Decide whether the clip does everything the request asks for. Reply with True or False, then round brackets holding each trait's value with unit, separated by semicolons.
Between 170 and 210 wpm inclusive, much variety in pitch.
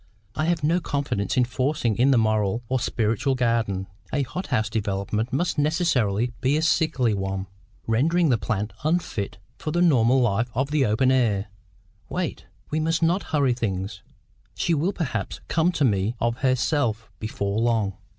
False (160 wpm; 5.9 semitones)